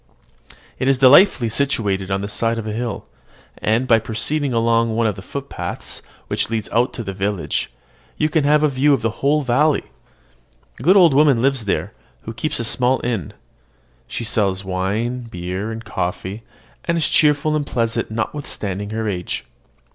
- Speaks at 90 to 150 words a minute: No, average, 175 wpm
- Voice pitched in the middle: No, low, 115 Hz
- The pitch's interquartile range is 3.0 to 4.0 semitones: No, average, 4.9 semitones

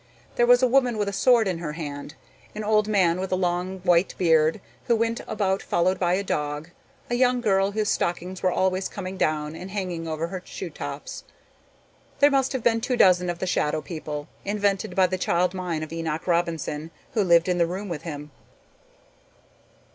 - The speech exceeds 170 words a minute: Yes, average, 195 wpm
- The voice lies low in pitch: No, medium, 185 Hz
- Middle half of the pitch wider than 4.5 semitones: No, average, 3.7 semitones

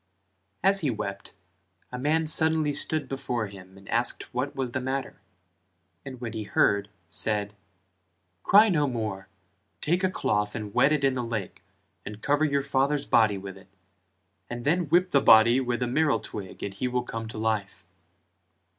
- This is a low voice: Yes, low, 125 Hz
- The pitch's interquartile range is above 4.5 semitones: Yes, wide, 5.6 semitones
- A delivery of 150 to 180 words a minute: Yes, average, 170 wpm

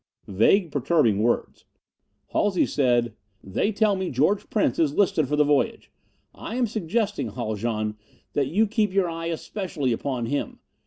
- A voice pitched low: No, medium, 155 Hz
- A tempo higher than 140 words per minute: Yes, average, 150 wpm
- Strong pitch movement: Yes, wide, 8.4 semitones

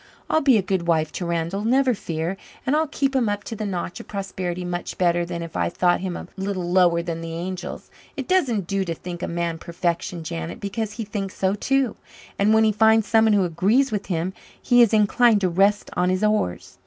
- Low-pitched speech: No, high, 190 Hz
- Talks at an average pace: No, fast, 225 wpm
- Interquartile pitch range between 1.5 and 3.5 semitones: No, average, 4.0 semitones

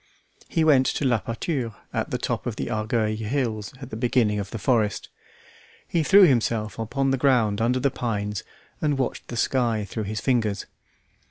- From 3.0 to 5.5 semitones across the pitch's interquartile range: Yes, average, 3.6 semitones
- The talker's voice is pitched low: Yes, low, 115 Hz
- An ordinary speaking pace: Yes, average, 180 wpm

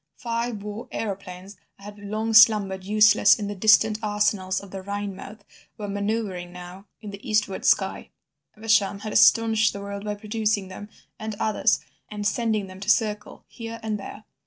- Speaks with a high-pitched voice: Yes, high, 210 Hz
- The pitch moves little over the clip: Yes, narrow, 1.6 semitones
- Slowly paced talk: No, average, 165 wpm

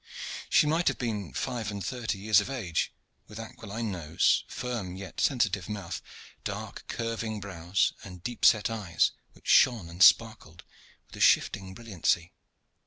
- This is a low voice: Yes, low, 105 Hz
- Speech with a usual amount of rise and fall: Yes, average, 3.8 semitones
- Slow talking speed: No, average, 150 wpm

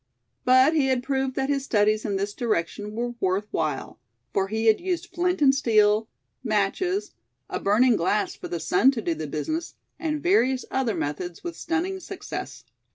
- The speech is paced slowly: No, average, 175 wpm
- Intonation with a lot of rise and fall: Yes, wide, 6.6 semitones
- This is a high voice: Yes, high, 245 Hz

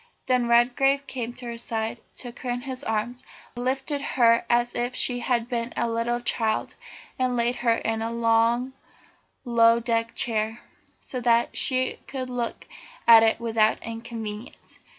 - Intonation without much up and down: Yes, narrow, 1.4 semitones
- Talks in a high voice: Yes, high, 235 Hz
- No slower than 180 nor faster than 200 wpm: No, average, 155 wpm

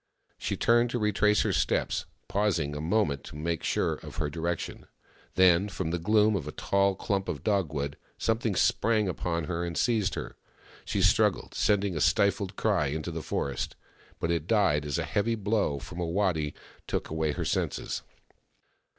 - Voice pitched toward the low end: Yes, very low, 90 Hz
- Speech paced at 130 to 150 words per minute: No, average, 175 wpm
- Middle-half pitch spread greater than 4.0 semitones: Yes, average, 4.7 semitones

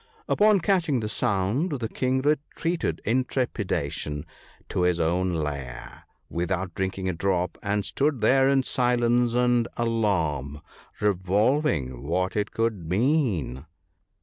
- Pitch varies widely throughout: Yes, wide, 6.5 semitones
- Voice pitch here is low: Yes, low, 105 Hz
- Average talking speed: No, slow, 120 wpm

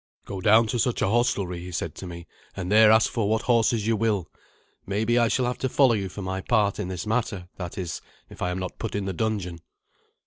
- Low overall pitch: Yes, low, 105 Hz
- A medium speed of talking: No, fast, 240 wpm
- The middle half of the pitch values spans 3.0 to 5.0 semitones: Yes, average, 3.6 semitones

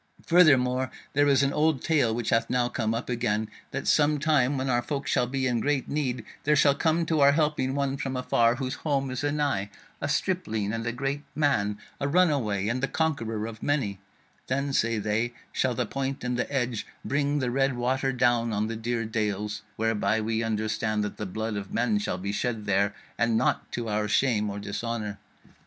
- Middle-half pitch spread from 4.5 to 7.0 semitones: No, average, 4.1 semitones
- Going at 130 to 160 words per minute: No, average, 200 wpm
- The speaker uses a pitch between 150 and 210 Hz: No, low, 125 Hz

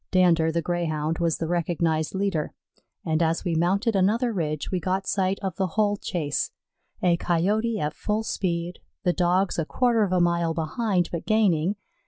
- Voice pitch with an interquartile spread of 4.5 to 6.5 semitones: No, average, 3.2 semitones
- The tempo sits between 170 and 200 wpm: Yes, average, 175 wpm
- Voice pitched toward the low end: No, medium, 175 Hz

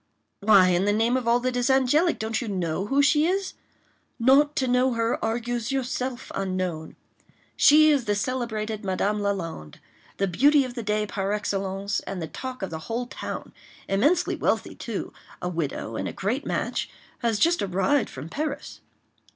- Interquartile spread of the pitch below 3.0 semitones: No, average, 5.1 semitones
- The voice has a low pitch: No, high, 225 Hz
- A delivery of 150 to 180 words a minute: Yes, average, 165 wpm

